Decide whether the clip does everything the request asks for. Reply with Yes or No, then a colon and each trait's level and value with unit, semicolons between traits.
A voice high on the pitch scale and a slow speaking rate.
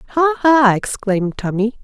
Yes: high, 245 Hz; slow, 130 wpm